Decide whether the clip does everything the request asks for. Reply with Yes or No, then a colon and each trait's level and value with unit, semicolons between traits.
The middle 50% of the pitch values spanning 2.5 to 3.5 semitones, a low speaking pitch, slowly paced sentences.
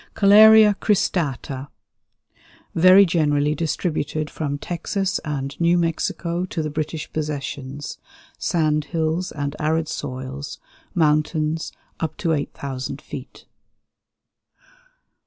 No: average, 2.8 semitones; medium, 155 Hz; slow, 95 wpm